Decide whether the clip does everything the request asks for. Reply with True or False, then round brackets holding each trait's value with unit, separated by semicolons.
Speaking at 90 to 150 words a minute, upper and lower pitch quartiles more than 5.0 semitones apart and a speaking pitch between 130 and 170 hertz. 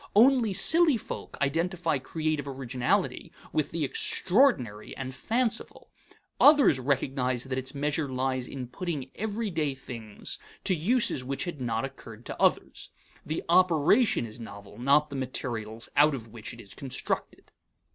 True (140 wpm; 5.5 semitones; 140 Hz)